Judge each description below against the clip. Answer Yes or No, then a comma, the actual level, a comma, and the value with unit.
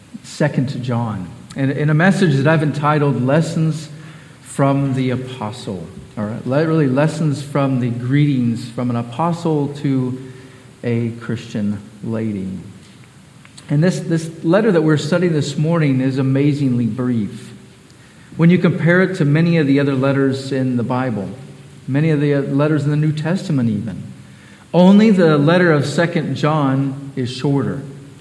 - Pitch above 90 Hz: Yes, medium, 140 Hz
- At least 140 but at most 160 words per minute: Yes, average, 150 wpm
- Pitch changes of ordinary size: Yes, average, 3.5 semitones